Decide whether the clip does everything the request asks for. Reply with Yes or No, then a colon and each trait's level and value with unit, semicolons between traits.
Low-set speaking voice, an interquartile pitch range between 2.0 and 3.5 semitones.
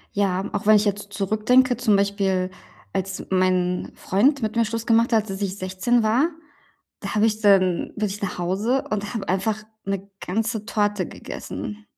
No: high, 205 Hz; narrow, 2.6 semitones